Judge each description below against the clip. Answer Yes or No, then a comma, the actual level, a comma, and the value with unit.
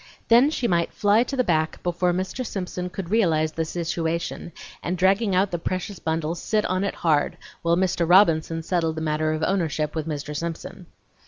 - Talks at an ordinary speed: Yes, average, 185 wpm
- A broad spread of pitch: No, average, 3.0 semitones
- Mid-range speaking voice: Yes, medium, 170 Hz